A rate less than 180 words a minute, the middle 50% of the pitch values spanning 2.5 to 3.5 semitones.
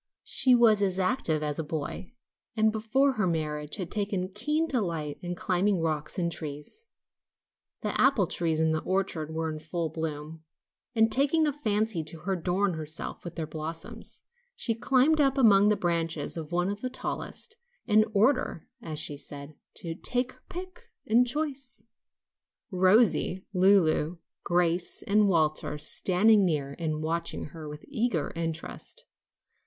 No: average, 150 wpm; wide, 5.6 semitones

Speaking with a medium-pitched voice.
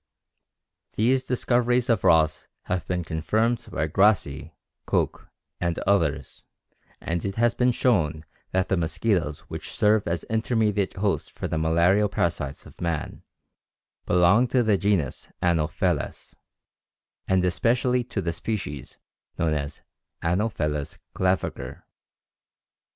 No: very low, 90 Hz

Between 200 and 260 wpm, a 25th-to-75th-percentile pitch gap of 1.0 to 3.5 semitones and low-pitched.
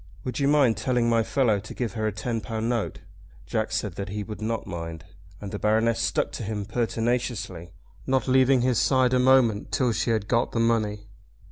Yes: fast, 205 wpm; average, 2.9 semitones; low, 115 Hz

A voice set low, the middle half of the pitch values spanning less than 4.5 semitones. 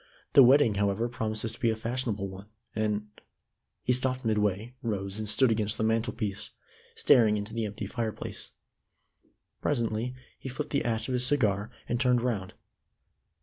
Yes: low, 110 Hz; average, 2.8 semitones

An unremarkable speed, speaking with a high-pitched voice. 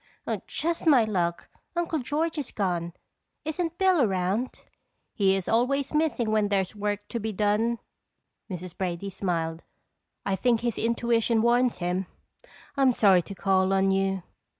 Yes: average, 145 wpm; high, 210 Hz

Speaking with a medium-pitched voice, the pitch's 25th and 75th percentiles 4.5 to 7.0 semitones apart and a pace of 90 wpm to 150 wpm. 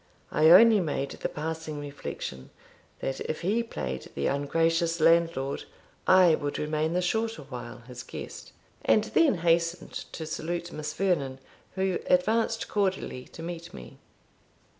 No: medium, 165 Hz; average, 3.4 semitones; average, 140 wpm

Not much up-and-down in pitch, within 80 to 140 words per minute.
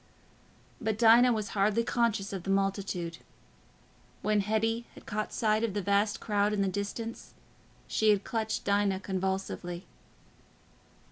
Yes: narrow, 2.1 semitones; slow, 135 wpm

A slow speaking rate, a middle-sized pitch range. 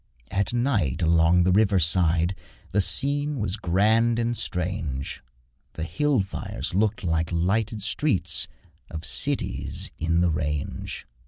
Yes: slow, 130 wpm; average, 5.0 semitones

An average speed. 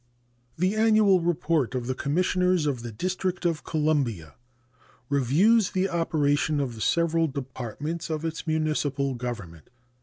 No: slow, 130 wpm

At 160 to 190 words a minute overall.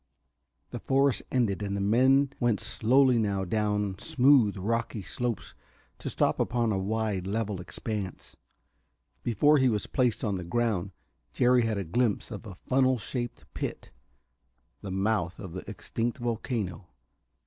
No: average, 145 wpm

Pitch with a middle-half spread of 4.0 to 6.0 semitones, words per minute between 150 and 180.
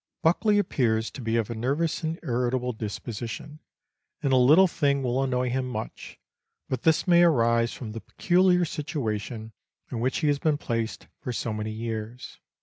Yes: average, 4.8 semitones; average, 170 wpm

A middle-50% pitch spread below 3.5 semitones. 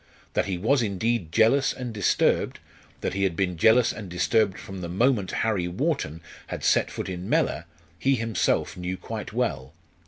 No: average, 4.4 semitones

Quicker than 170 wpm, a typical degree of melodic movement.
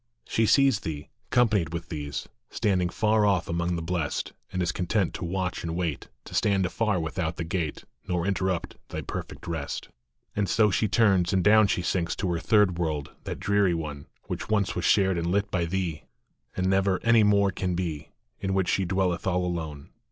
Yes: average, 195 wpm; average, 3.0 semitones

